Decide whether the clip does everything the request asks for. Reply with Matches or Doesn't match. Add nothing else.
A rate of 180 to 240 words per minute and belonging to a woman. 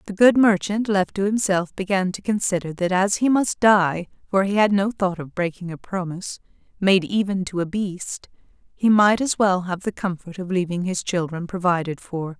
Matches